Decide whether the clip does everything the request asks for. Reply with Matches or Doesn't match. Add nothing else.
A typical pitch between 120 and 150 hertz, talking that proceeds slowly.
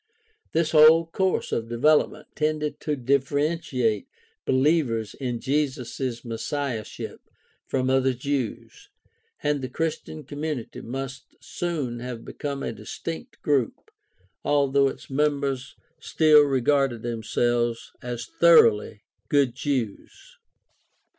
Matches